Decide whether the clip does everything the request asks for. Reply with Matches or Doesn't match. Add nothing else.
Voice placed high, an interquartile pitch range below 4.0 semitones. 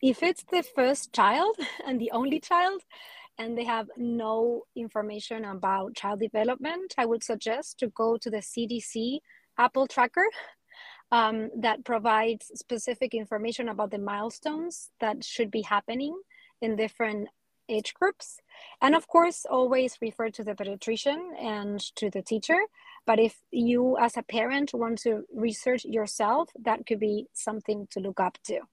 Matches